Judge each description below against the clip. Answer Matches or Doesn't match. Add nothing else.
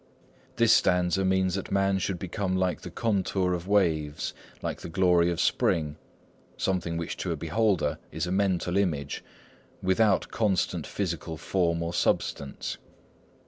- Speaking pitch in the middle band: Doesn't match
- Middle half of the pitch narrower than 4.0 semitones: Matches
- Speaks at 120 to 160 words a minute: Matches